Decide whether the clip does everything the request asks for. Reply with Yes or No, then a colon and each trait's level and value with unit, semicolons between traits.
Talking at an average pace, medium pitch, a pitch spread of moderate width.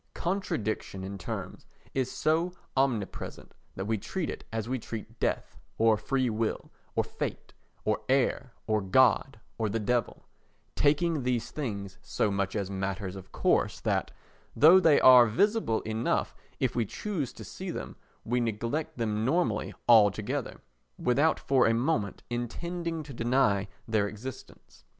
No: average, 145 wpm; low, 120 Hz; average, 4.4 semitones